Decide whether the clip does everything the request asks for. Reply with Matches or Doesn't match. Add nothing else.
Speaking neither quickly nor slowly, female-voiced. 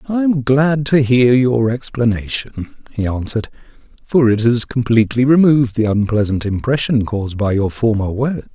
Doesn't match